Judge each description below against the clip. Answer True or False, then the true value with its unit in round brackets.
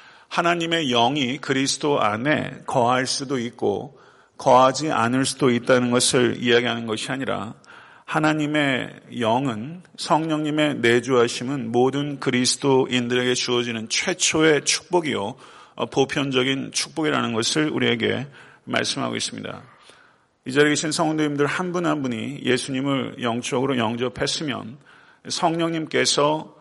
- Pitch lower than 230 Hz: True (135 Hz)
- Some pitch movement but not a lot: True (3.7 semitones)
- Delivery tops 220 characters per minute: True (300 characters per minute)